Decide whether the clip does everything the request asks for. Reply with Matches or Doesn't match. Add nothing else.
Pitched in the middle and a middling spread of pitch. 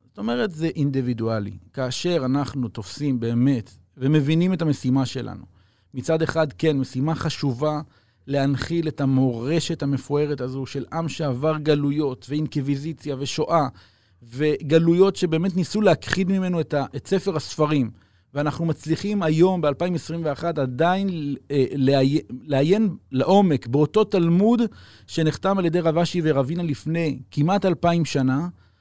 Matches